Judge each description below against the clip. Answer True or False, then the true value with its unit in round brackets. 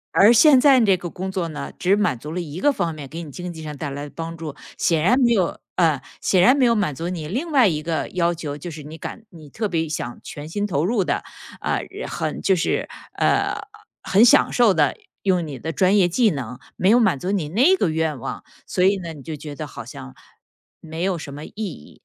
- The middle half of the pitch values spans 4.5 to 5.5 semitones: True (4.8 semitones)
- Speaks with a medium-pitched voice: True (170 Hz)